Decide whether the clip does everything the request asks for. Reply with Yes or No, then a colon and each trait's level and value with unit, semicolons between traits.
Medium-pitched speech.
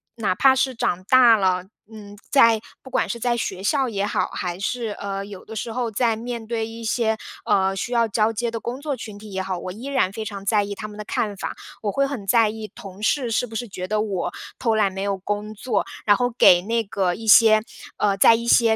No: high, 220 Hz